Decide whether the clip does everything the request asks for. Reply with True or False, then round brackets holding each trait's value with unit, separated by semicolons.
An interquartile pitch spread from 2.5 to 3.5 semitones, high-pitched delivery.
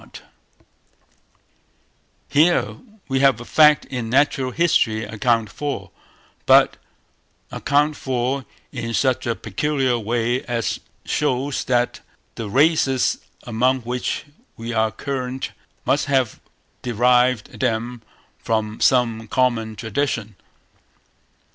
False (2.8 semitones; 125 Hz)